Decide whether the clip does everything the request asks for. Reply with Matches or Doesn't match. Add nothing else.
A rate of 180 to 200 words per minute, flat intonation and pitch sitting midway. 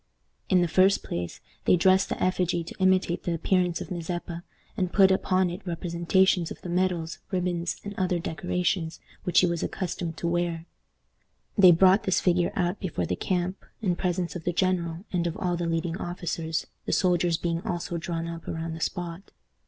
Matches